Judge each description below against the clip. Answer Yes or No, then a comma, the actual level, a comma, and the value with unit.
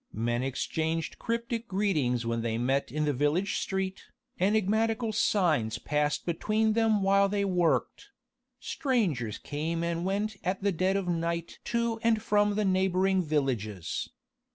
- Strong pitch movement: Yes, wide, 6.0 semitones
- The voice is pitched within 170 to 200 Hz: Yes, medium, 185 Hz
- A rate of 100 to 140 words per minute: Yes, slow, 135 wpm